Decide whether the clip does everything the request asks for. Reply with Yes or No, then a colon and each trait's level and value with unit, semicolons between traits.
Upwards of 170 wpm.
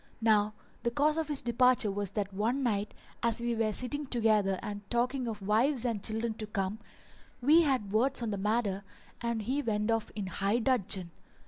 Yes: average, 190 wpm